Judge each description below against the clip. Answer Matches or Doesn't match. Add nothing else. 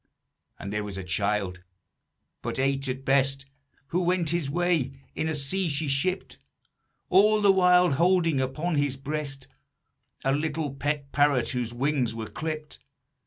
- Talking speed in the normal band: Matches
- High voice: Doesn't match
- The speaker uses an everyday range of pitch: Matches